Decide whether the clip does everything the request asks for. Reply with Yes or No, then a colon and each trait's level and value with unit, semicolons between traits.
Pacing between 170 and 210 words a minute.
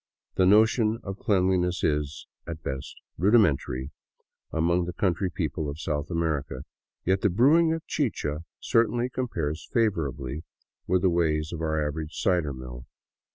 No: average, 140 wpm